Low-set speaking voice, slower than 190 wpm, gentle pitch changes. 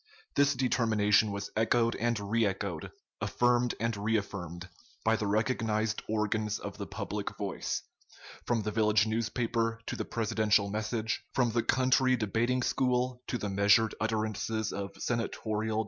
Yes: low, 110 Hz; average, 140 wpm; narrow, 1.9 semitones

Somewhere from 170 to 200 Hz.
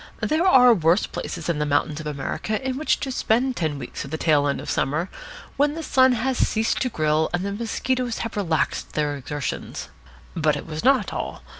Yes: medium, 185 Hz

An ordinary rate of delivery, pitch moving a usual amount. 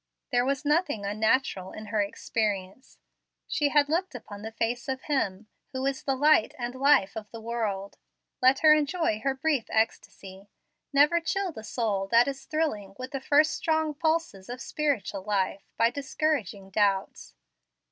No: average, 160 wpm; wide, 5.9 semitones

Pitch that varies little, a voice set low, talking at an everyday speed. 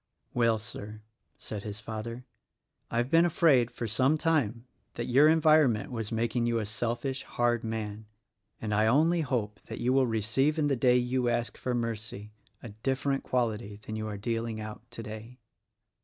No: average, 3.0 semitones; low, 120 Hz; average, 170 wpm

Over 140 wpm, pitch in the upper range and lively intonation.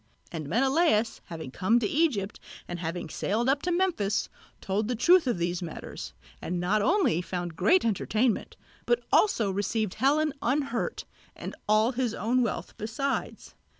Yes: average, 150 wpm; high, 225 Hz; wide, 6.5 semitones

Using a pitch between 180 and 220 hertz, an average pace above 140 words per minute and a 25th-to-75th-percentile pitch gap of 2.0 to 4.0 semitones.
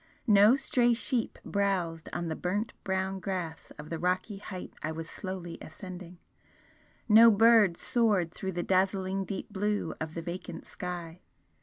Yes: high, 190 Hz; average, 150 wpm; average, 3.1 semitones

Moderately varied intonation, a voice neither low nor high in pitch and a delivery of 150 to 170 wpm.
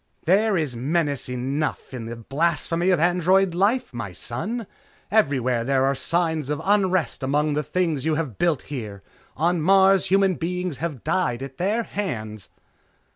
No: wide, 5.7 semitones; medium, 160 Hz; average, 155 wpm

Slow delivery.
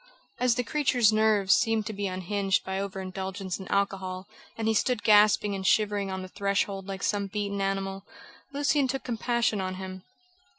No: average, 175 wpm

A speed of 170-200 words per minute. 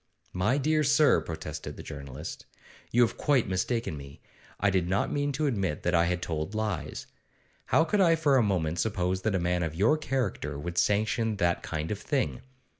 Yes: average, 190 wpm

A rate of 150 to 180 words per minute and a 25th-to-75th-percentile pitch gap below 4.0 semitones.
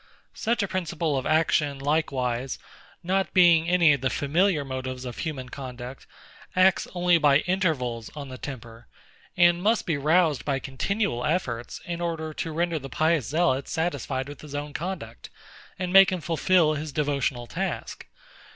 No: average, 160 wpm; average, 4.6 semitones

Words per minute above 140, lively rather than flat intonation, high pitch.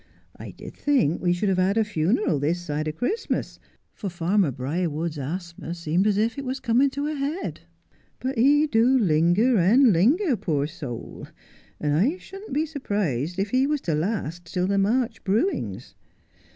Yes: average, 180 wpm; wide, 7.6 semitones; high, 200 Hz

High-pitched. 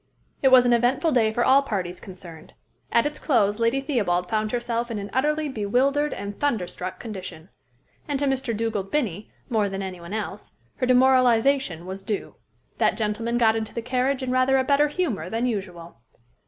Yes: high, 230 Hz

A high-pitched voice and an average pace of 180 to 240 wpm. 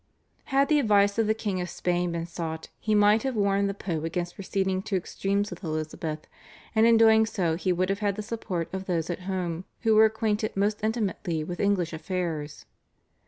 Yes: high, 195 Hz; average, 200 wpm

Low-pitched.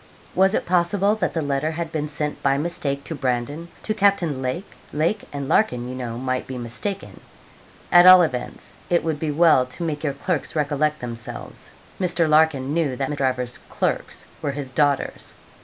No: medium, 150 Hz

